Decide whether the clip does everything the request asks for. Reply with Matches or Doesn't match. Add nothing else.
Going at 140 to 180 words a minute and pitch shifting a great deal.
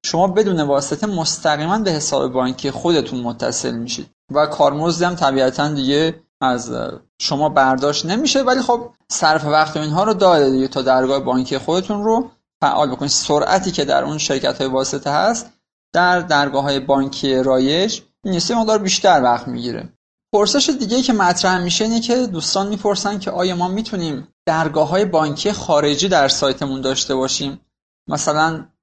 Matches